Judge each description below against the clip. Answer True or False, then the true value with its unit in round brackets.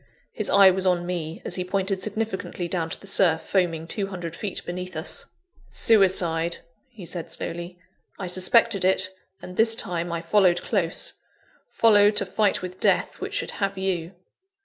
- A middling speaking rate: True (170 wpm)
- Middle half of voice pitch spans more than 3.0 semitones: False (2.4 semitones)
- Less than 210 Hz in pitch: True (185 Hz)